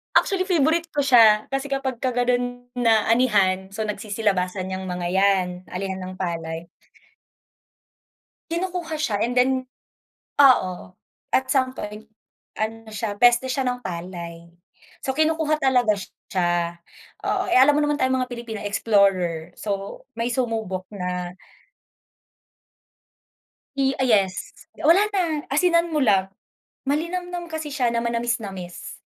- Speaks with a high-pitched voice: Yes, high, 230 Hz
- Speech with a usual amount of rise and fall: No, wide, 6.2 semitones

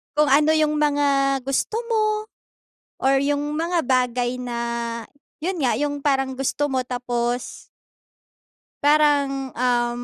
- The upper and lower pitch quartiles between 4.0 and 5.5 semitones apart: No, average, 2.7 semitones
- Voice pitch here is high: Yes, very high, 275 Hz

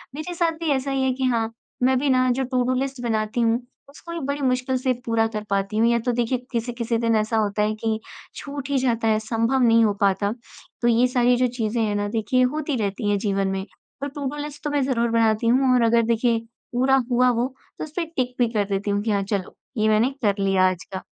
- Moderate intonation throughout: Yes, average, 3.3 semitones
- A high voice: Yes, high, 235 Hz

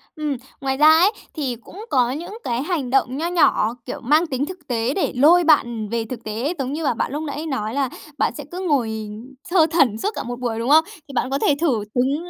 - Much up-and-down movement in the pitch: No, average, 4.6 semitones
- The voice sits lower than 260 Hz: No, very high, 275 Hz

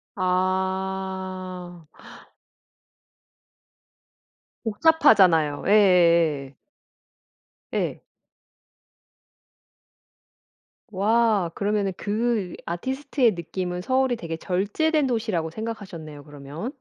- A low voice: No, high, 190 Hz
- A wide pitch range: No, average, 4.3 semitones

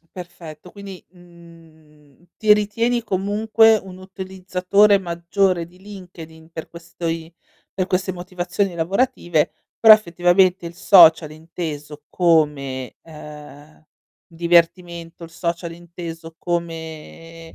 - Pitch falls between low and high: Yes, medium, 170 Hz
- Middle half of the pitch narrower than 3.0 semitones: Yes, narrow, 2.5 semitones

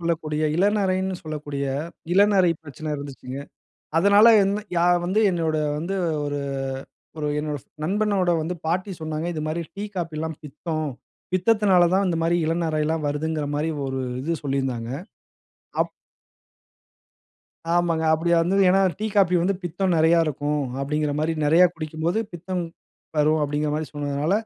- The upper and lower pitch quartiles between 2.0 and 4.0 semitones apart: Yes, average, 3.3 semitones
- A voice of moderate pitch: Yes, medium, 160 Hz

